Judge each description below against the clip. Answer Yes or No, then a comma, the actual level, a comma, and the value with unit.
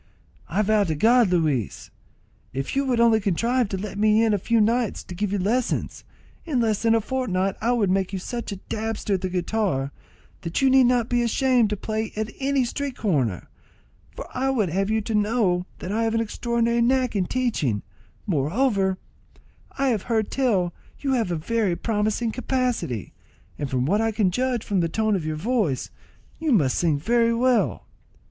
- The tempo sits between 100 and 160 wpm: No, average, 195 wpm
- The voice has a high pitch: Yes, high, 215 Hz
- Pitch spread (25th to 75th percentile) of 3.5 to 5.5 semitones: Yes, average, 4.5 semitones